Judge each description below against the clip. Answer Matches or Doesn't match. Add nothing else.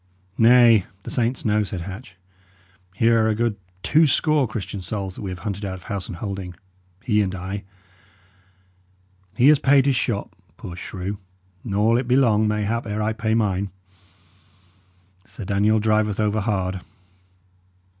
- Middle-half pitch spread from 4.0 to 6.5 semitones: Doesn't match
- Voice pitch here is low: Matches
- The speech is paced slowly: Doesn't match